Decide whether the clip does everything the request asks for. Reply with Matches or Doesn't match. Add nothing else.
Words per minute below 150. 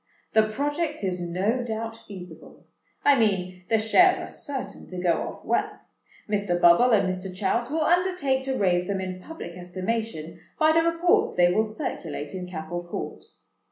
Doesn't match